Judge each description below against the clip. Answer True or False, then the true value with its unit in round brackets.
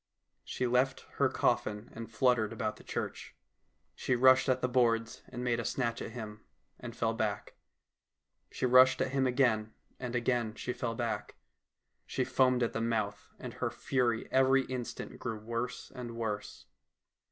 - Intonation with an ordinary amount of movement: False (2.0 semitones)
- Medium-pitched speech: False (120 Hz)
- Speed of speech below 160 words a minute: False (165 wpm)